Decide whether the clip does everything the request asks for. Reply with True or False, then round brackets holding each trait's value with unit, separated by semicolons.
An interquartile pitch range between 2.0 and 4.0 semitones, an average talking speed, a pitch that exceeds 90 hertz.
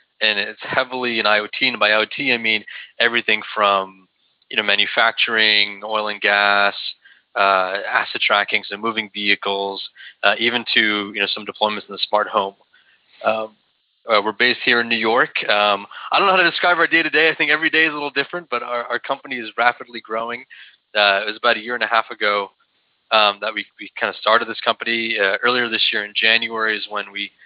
False (2.9 semitones; 210 wpm; 110 Hz)